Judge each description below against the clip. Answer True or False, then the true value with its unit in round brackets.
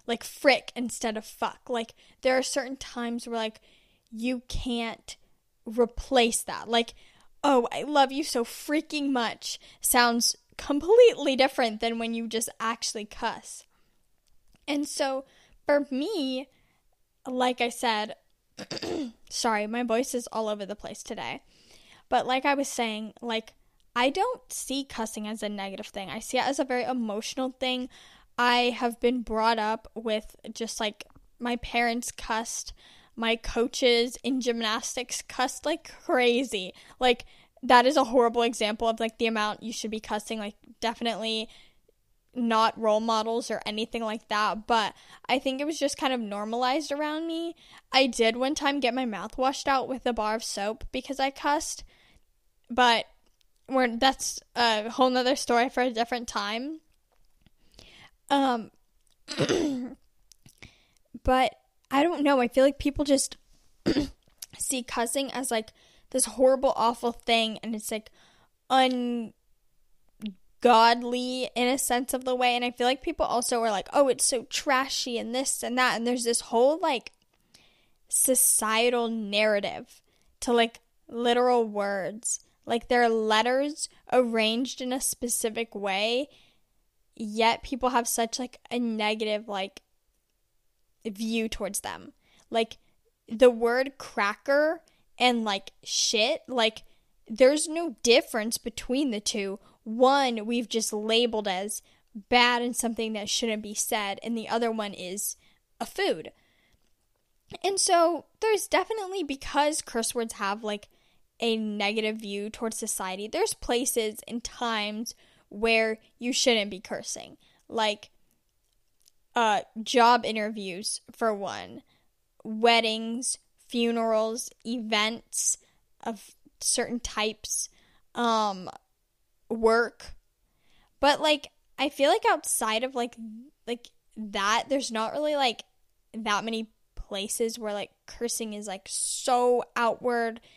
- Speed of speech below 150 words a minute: True (135 wpm)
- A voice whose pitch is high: True (235 Hz)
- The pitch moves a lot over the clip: False (2.7 semitones)